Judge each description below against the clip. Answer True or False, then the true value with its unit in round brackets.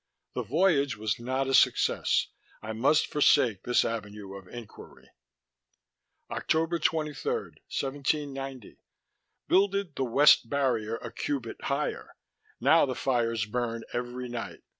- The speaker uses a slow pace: True (120 wpm)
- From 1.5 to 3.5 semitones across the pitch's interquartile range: False (4.0 semitones)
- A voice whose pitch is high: False (130 Hz)